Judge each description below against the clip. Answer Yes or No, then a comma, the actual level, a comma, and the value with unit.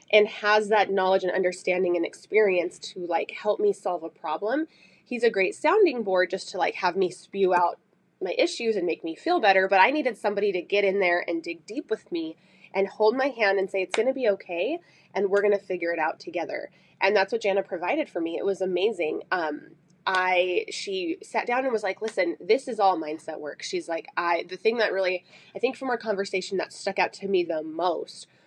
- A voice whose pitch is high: Yes, high, 195 Hz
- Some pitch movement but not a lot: Yes, average, 3.3 semitones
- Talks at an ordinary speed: No, fast, 230 wpm